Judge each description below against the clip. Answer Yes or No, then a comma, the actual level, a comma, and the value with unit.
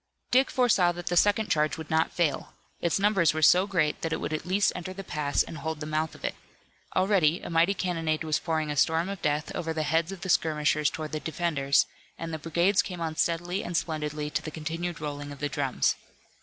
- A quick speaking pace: Yes, fast, 225 wpm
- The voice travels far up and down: No, narrow, 2.6 semitones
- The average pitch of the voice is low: No, medium, 160 Hz